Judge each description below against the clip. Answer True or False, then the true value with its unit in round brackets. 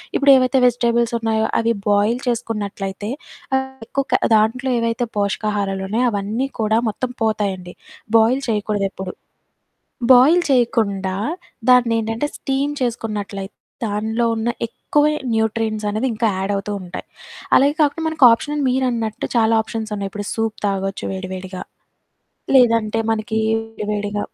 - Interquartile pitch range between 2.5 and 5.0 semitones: True (3.0 semitones)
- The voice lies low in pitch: False (220 Hz)